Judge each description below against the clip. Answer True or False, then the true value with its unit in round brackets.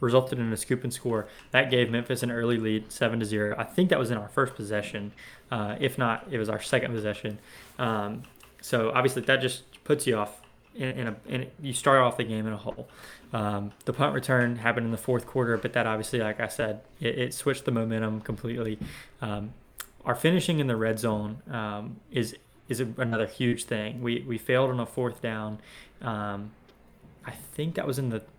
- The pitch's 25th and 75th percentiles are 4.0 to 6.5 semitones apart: False (2.9 semitones)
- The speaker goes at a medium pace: False (210 wpm)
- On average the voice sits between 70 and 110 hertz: False (120 Hz)